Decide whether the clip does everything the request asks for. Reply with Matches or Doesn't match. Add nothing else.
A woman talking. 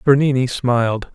Doesn't match